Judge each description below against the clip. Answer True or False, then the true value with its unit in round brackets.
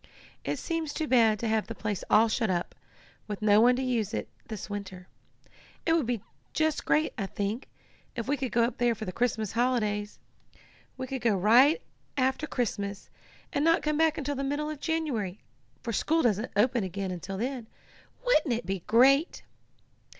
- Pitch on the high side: True (235 Hz)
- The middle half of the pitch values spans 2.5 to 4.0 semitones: False (5.1 semitones)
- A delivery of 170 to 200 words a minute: True (185 wpm)